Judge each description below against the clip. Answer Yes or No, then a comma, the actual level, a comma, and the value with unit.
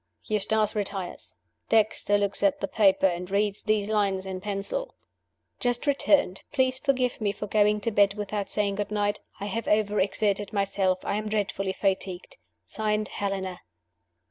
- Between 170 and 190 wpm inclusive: No, average, 150 wpm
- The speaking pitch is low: No, high, 205 Hz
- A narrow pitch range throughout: Yes, narrow, 1.6 semitones